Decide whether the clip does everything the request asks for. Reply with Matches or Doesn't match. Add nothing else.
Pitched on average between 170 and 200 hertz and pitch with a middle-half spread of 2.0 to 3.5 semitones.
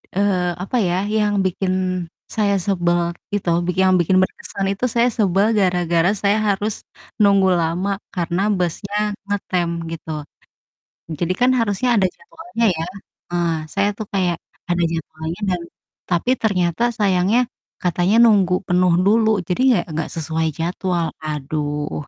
Matches